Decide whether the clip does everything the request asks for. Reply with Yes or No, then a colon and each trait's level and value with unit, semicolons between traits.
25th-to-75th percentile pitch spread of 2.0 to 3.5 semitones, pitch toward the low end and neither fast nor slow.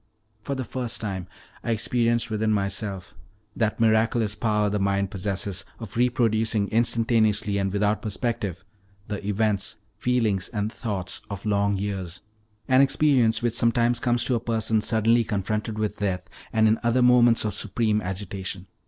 Yes: narrow, 2.6 semitones; low, 110 Hz; average, 150 wpm